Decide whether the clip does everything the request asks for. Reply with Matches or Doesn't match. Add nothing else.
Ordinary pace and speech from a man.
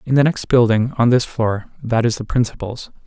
Matches